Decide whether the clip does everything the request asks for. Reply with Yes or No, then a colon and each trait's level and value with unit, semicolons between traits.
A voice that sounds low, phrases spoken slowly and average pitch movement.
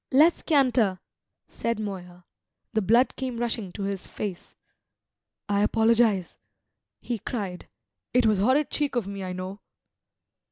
No: high, 215 Hz; slow, 130 wpm; average, 4.0 semitones